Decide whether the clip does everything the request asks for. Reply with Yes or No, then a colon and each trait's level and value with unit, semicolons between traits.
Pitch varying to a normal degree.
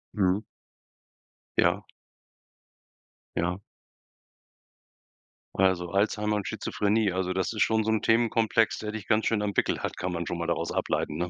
Yes: average, 3.2 semitones